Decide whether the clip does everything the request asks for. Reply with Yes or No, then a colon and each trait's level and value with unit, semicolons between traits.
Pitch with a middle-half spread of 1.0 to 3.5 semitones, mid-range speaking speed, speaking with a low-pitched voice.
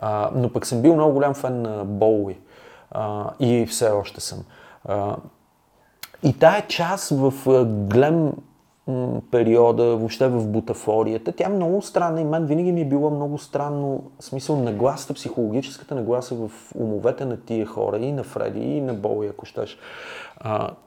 No: average, 4.9 semitones; average, 150 wpm; low, 125 Hz